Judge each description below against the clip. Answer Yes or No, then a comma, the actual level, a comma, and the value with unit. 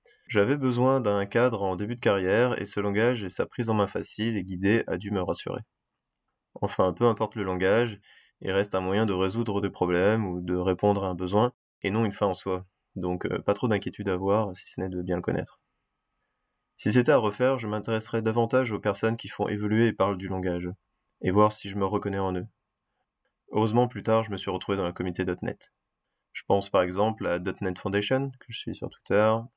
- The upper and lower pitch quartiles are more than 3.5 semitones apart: No, average, 3.1 semitones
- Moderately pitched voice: No, low, 100 Hz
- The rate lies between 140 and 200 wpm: No, fast, 220 wpm